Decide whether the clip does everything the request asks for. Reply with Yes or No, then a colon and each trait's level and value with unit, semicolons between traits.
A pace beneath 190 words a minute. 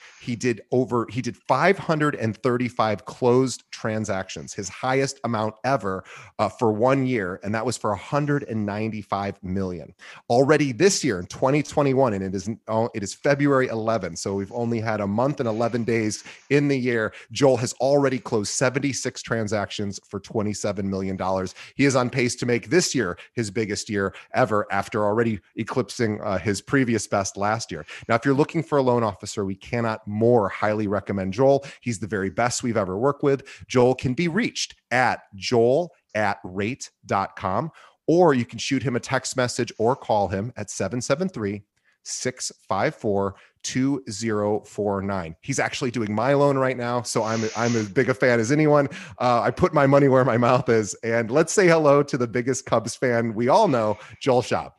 Yes: average, 175 wpm